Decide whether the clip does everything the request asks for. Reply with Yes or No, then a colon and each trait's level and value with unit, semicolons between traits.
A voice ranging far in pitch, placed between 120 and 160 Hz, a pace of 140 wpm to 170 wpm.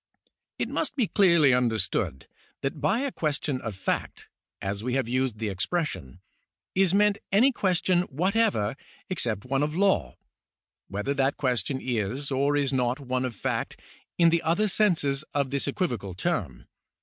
Yes: wide, 6.5 semitones; medium, 140 Hz; average, 160 wpm